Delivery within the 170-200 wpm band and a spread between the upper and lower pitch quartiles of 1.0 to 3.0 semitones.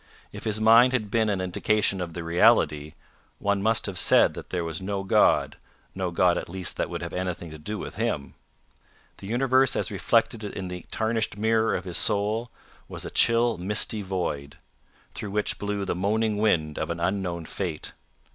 No: average, 185 wpm; average, 3.7 semitones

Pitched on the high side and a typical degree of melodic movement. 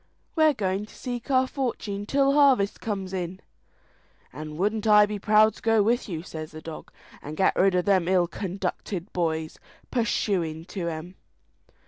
Yes: high, 195 Hz; average, 4.2 semitones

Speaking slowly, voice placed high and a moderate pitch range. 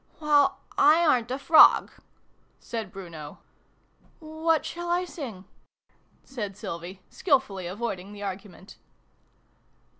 No: slow, 120 wpm; high, 230 Hz; wide, 8.1 semitones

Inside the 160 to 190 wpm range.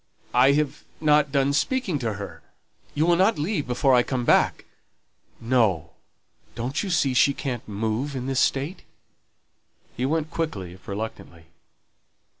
No: average, 145 wpm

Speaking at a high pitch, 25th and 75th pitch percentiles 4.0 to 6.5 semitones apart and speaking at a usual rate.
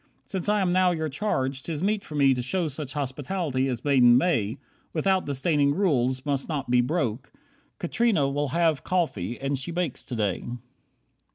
No: medium, 145 Hz; average, 5.0 semitones; average, 170 wpm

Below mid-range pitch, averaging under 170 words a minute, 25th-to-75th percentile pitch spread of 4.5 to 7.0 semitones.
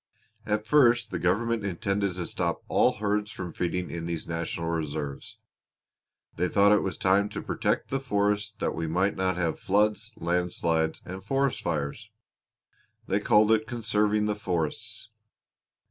No: low, 100 Hz; average, 150 wpm; average, 3.8 semitones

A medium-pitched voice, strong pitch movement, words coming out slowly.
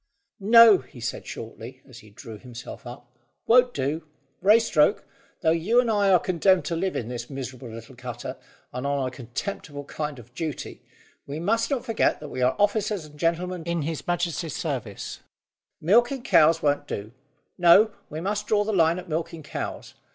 No: medium, 160 Hz; wide, 7.4 semitones; average, 175 wpm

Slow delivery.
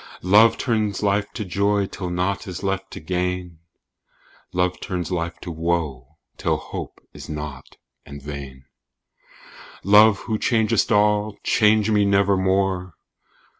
Yes: slow, 130 wpm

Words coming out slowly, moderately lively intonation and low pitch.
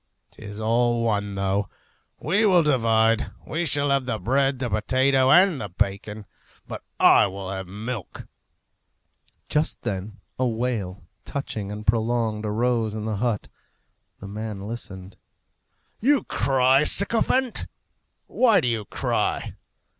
Yes: slow, 130 wpm; average, 4.5 semitones; low, 115 Hz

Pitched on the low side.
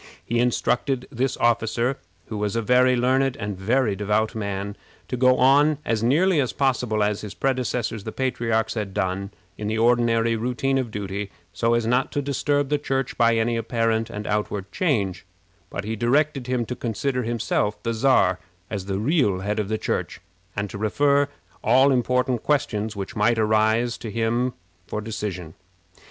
Yes: low, 115 Hz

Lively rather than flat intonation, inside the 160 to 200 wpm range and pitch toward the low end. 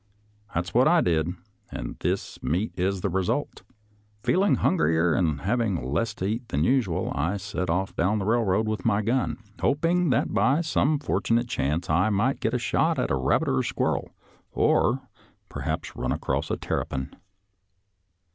Yes: wide, 5.9 semitones; average, 170 wpm; low, 100 Hz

